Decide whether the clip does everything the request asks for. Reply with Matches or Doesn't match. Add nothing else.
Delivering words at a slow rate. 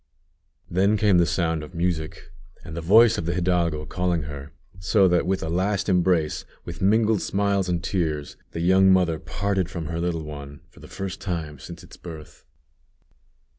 Doesn't match